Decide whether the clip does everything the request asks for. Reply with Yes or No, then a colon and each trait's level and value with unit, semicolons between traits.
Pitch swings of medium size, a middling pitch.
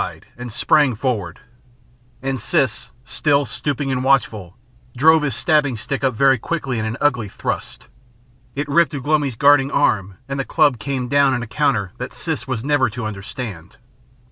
No: average, 4.0 semitones; low, 130 Hz